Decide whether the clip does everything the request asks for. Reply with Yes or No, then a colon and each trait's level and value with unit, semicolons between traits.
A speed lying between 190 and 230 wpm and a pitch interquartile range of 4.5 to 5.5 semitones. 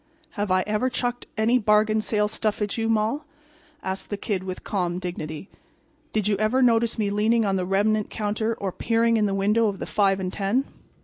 No: average, 200 wpm; narrow, 2.5 semitones